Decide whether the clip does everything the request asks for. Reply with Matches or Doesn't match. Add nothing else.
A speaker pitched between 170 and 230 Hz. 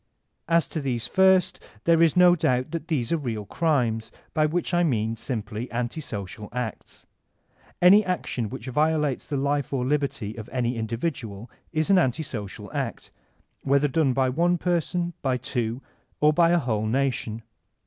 Doesn't match